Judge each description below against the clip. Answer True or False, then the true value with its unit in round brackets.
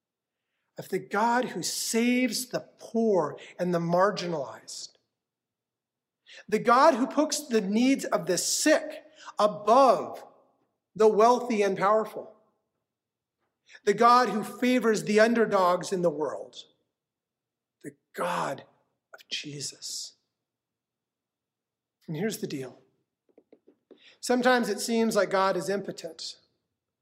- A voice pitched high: True (210 Hz)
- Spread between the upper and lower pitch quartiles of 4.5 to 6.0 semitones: True (5.1 semitones)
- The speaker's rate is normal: False (105 wpm)